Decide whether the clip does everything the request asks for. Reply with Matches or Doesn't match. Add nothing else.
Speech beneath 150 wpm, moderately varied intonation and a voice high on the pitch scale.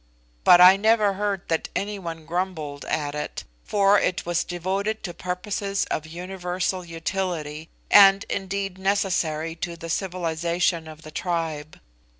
Doesn't match